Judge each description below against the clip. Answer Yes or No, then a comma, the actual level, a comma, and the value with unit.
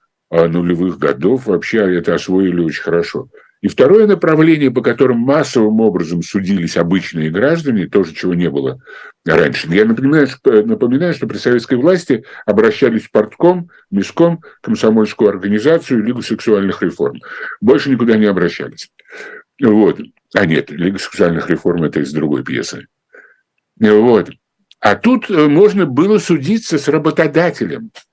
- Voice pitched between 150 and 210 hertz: No, low, 135 Hz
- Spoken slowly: No, average, 130 wpm